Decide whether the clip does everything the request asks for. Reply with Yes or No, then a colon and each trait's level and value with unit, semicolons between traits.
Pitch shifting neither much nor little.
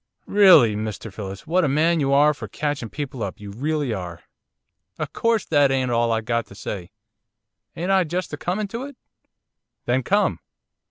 No: wide, 7.5 semitones